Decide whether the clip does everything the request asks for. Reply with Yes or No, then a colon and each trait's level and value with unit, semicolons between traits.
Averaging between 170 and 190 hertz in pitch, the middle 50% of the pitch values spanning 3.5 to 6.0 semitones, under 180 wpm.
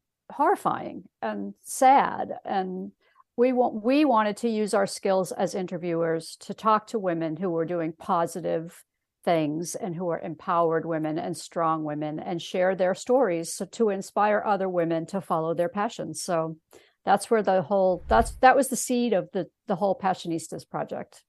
Yes: medium, 185 Hz; average, 3.9 semitones; average, 170 wpm